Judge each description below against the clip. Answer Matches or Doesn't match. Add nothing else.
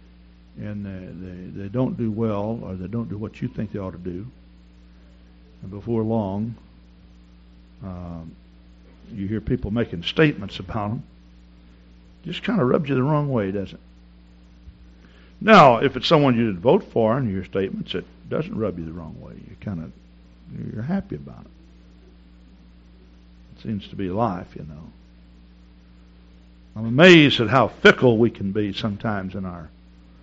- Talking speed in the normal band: Matches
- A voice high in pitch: Doesn't match